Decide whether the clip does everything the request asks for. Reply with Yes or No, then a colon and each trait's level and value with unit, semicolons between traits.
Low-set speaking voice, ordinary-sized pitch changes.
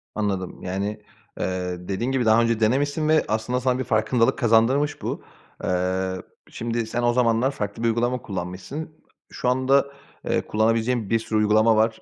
Yes: low, 115 Hz; average, 3.1 semitones